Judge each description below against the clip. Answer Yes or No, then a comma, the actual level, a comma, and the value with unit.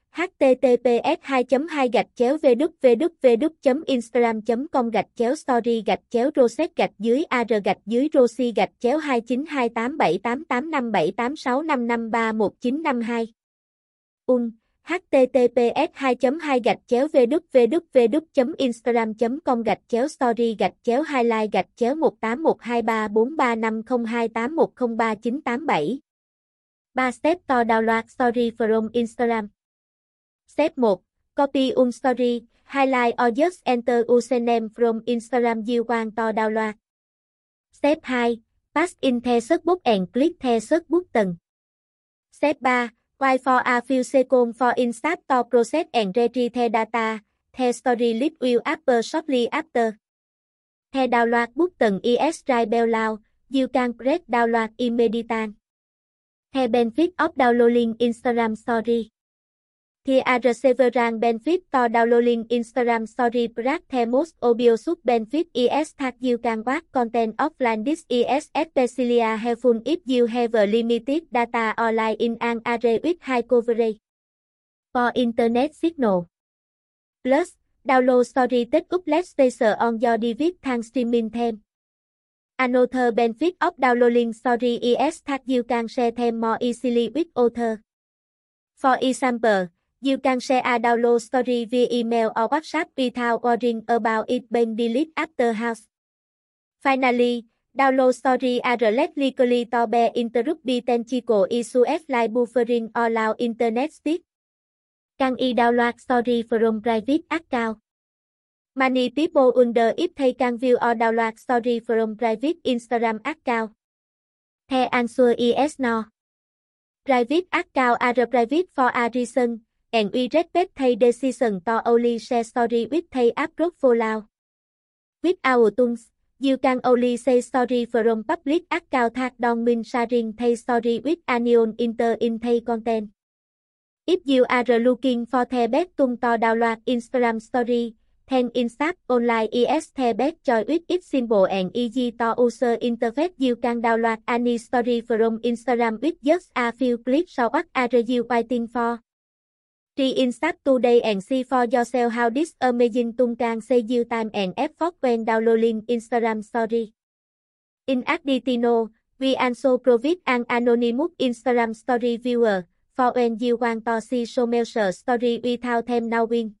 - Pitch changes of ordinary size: No, narrow, 2.0 semitones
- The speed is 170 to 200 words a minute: No, slow, 135 wpm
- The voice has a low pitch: No, high, 245 Hz